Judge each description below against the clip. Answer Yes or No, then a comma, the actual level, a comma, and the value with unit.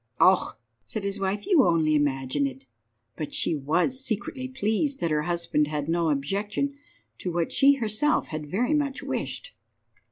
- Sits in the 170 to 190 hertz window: Yes, medium, 185 Hz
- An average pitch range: No, wide, 9.0 semitones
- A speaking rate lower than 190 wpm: Yes, average, 160 wpm